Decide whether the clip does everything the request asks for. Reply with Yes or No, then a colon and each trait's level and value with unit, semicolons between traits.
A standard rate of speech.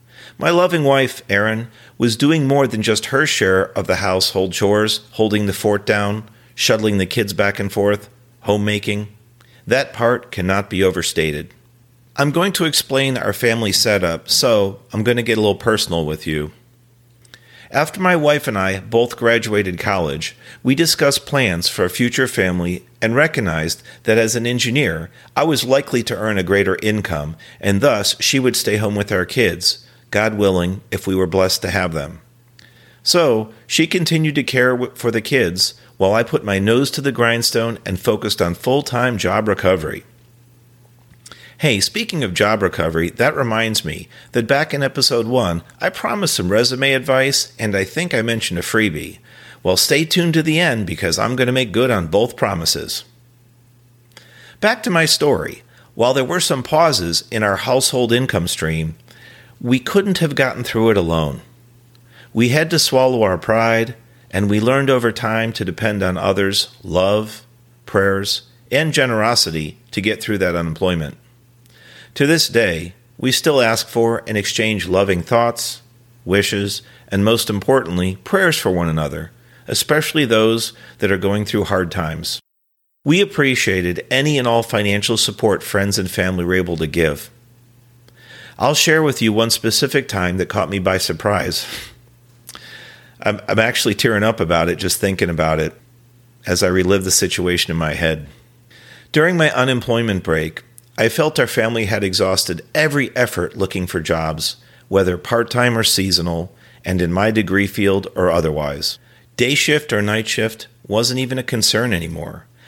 Yes: average, 165 wpm